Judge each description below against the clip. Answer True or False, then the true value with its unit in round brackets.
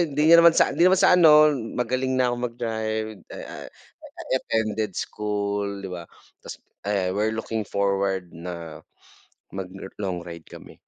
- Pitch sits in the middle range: False (110 Hz)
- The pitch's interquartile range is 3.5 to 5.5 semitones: True (4.2 semitones)